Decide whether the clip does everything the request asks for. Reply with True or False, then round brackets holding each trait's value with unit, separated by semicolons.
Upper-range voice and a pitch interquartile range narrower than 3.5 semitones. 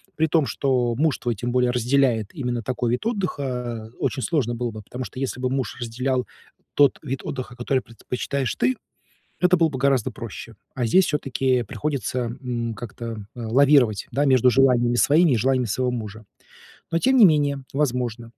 False (125 Hz; 2.7 semitones)